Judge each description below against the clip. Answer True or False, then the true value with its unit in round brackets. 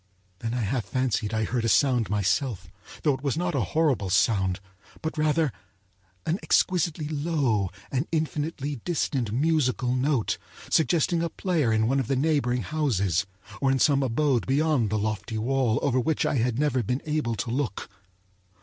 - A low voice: True (130 Hz)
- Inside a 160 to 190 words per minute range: True (170 wpm)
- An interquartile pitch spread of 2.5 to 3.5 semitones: False (5.1 semitones)